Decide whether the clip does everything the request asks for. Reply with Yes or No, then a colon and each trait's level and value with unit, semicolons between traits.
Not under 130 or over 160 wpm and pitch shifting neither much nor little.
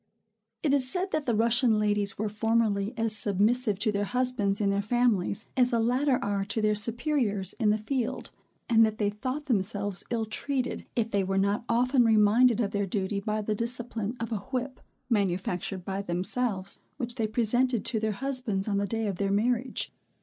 No: average, 190 wpm; average, 3.3 semitones